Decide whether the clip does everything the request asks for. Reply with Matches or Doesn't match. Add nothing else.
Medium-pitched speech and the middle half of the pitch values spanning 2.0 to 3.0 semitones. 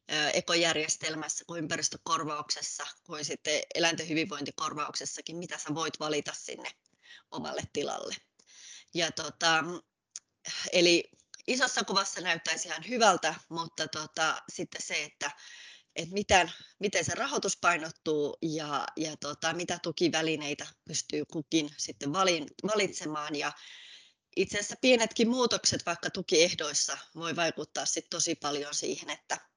Matches